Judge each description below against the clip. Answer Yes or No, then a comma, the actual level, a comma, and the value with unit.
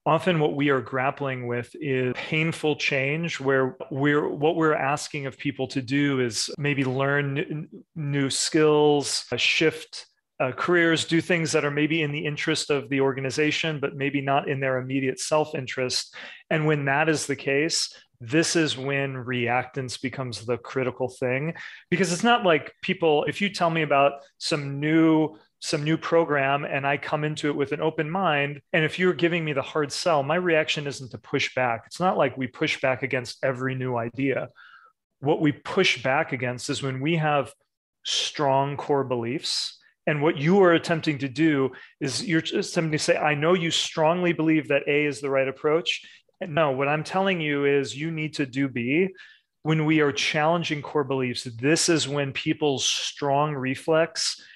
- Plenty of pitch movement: No, average, 2.9 semitones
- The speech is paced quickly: No, average, 185 wpm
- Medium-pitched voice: Yes, medium, 145 Hz